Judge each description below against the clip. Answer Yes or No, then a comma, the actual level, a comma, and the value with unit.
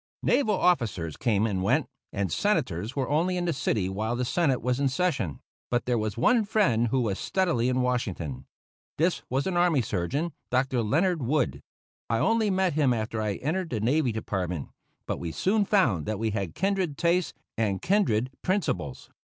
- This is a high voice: No, low, 125 Hz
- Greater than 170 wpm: Yes, average, 180 wpm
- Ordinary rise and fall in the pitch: No, wide, 8.6 semitones